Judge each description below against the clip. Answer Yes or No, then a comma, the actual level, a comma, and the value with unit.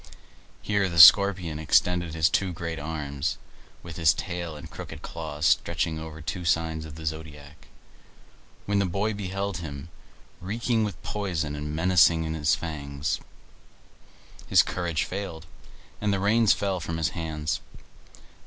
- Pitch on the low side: Yes, very low, 80 Hz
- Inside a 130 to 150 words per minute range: Yes, average, 145 wpm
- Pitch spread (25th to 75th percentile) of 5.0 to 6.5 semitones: No, average, 3.2 semitones